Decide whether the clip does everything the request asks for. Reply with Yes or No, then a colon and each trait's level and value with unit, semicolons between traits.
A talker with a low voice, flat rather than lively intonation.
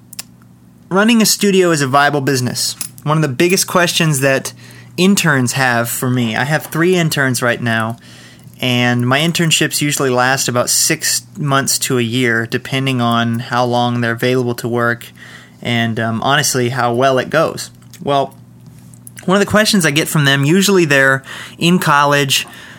No: low, 130 Hz; average, 4.4 semitones